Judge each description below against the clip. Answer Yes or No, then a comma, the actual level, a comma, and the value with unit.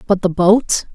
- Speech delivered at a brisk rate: No, average, 190 wpm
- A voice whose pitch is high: Yes, high, 195 Hz